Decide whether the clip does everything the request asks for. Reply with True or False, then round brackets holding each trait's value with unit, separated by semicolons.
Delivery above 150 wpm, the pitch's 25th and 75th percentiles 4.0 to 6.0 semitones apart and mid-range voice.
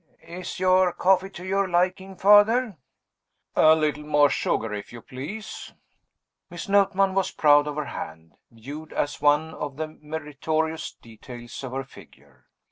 False (145 wpm; 4.5 semitones; 155 Hz)